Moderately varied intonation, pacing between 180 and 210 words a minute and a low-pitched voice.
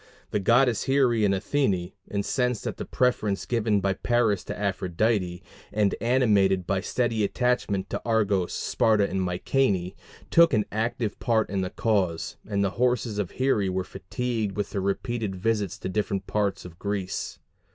No: average, 3.5 semitones; average, 160 wpm; low, 105 Hz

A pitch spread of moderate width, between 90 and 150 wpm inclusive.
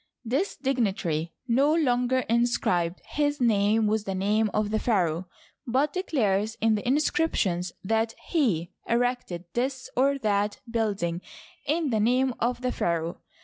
Yes: average, 4.5 semitones; average, 140 wpm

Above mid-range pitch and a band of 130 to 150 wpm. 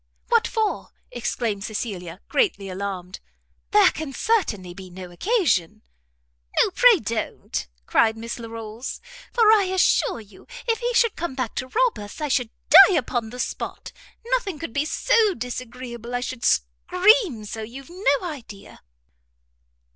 Yes: very high, 250 Hz; average, 145 wpm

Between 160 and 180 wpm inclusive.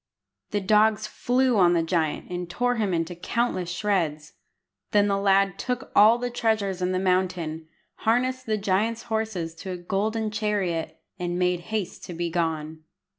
Yes: average, 165 wpm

